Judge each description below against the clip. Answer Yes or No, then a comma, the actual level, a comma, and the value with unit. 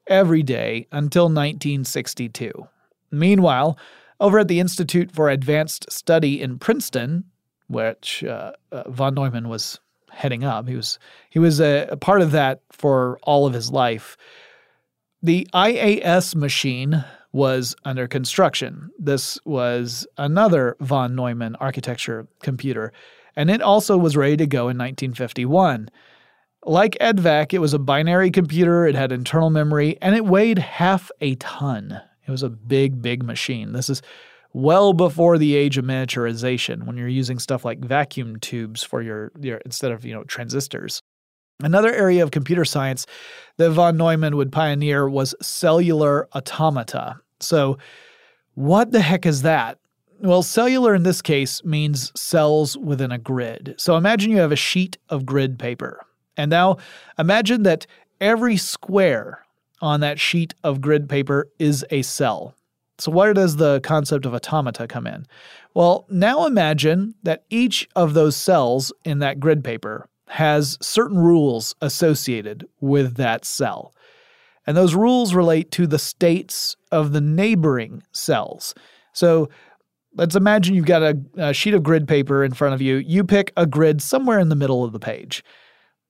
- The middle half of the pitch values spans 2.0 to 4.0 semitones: No, average, 4.9 semitones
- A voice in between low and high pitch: Yes, medium, 150 Hz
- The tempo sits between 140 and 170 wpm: Yes, average, 155 wpm